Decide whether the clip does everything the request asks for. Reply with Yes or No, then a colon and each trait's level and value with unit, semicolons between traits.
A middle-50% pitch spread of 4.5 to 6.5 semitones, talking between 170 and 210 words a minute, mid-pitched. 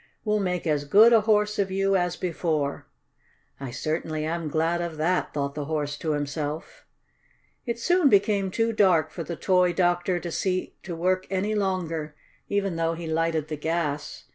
No: average, 3.6 semitones; average, 175 wpm; medium, 175 Hz